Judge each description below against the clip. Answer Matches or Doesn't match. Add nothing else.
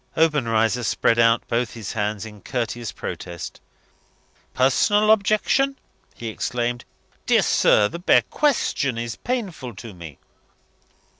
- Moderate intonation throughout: Doesn't match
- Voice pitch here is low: Matches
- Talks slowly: Matches